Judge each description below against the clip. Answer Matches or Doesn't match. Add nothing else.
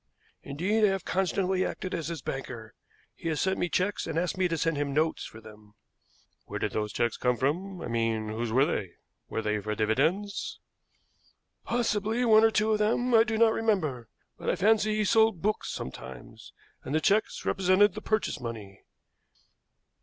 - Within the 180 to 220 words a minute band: Matches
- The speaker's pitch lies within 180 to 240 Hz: Doesn't match